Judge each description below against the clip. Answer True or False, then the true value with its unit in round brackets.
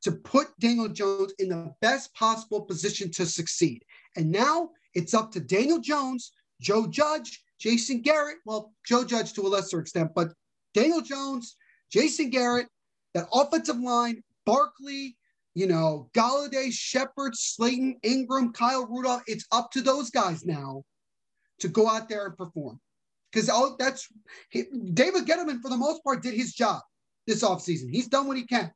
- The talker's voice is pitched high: True (235 Hz)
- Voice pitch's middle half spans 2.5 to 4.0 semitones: False (5.4 semitones)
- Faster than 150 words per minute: True (160 wpm)